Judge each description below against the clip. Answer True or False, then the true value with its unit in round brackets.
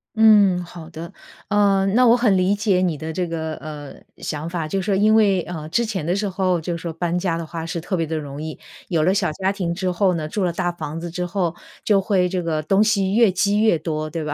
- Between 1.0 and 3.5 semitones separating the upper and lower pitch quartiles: True (3.2 semitones)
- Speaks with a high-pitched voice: False (180 Hz)